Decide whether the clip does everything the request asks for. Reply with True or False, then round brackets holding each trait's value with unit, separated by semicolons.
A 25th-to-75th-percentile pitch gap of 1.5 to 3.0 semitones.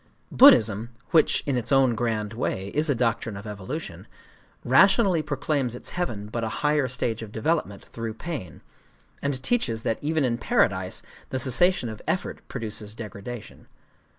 False (4.9 semitones)